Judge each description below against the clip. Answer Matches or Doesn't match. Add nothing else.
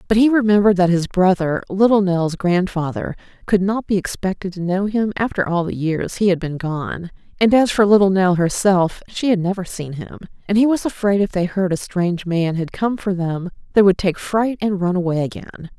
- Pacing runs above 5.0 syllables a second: Matches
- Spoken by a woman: Matches